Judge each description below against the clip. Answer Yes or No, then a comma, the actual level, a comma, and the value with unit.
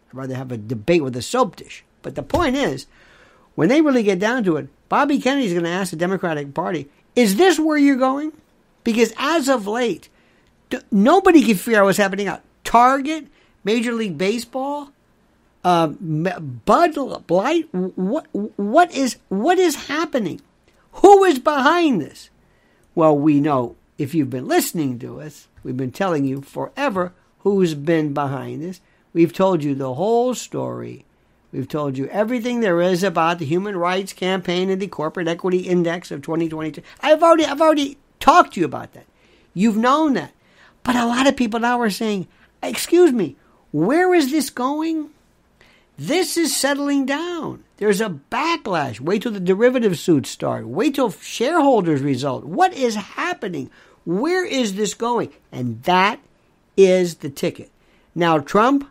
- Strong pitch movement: Yes, wide, 8.8 semitones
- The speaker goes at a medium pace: Yes, average, 165 wpm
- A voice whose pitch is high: Yes, high, 210 Hz